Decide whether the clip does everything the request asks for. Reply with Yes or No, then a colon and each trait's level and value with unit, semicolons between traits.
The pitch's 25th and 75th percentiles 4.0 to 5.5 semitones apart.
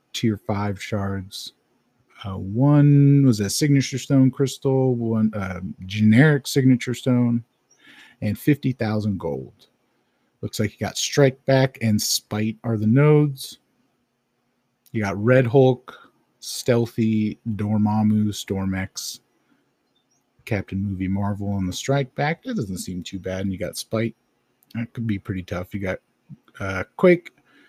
Yes: average, 4.3 semitones